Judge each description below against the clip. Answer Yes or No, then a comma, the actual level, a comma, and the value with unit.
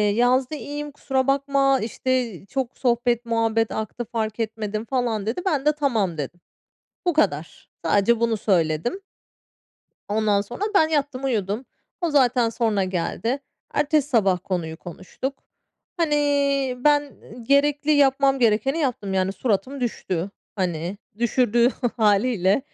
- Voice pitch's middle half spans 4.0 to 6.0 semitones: Yes, average, 5.2 semitones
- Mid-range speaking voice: No, high, 235 Hz